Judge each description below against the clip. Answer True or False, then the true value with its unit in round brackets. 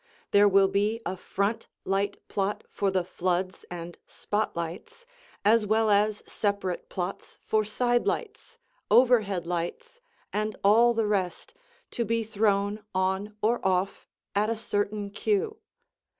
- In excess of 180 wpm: False (135 wpm)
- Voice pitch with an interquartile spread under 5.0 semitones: True (2.7 semitones)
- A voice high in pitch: True (205 Hz)